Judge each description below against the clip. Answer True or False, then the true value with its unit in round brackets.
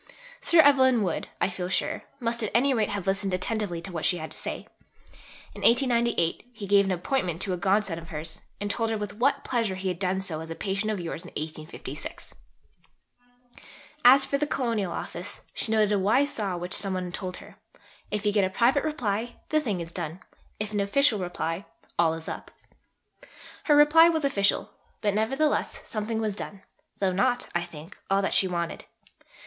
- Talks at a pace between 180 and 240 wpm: True (195 wpm)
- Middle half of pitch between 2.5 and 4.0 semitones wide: False (4.6 semitones)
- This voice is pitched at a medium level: False (200 Hz)